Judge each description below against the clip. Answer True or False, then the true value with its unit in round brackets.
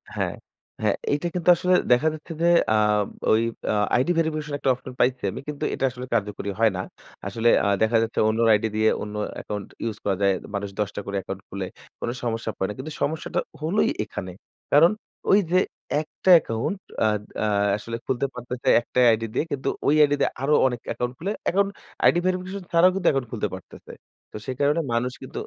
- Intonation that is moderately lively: False (6.1 semitones)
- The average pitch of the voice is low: True (125 Hz)